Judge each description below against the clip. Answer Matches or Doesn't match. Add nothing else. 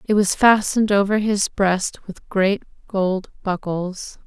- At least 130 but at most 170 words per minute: Matches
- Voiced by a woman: Matches